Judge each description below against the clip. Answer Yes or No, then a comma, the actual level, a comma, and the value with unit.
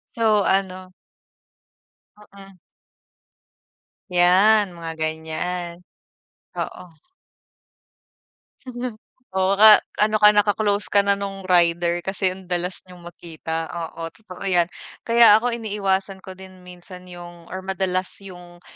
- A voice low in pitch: No, medium, 185 Hz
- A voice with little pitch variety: Yes, narrow, 2.2 semitones